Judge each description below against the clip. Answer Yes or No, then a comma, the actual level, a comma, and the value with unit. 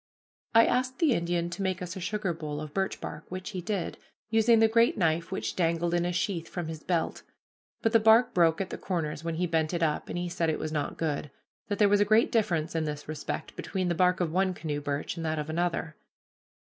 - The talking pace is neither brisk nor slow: No, fast, 240 wpm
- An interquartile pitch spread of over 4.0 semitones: No, average, 3.4 semitones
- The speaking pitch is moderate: Yes, medium, 175 Hz